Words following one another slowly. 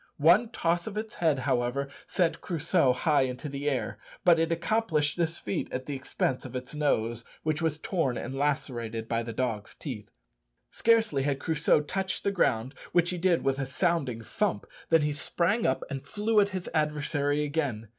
No: average, 185 wpm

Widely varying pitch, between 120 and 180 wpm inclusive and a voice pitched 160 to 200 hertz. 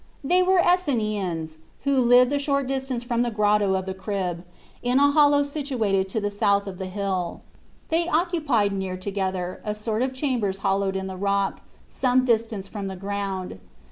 No: wide, 5.7 semitones; average, 175 wpm; high, 210 Hz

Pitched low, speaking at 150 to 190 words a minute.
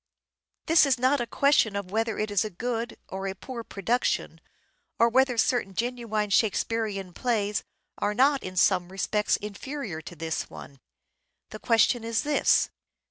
No: high, 220 Hz; average, 160 wpm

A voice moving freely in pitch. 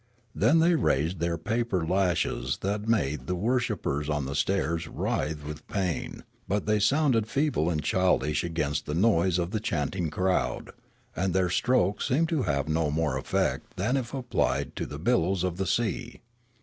Yes: wide, 6.0 semitones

